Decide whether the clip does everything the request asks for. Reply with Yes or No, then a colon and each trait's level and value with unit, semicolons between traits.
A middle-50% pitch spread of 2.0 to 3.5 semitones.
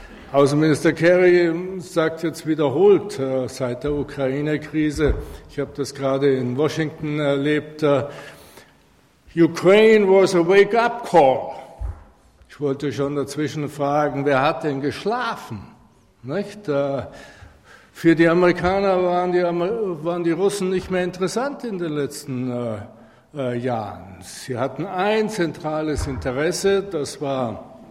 No: average, 4.6 semitones